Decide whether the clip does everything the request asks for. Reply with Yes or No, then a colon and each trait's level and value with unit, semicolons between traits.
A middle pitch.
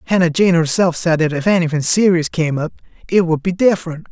Yes: medium, 165 Hz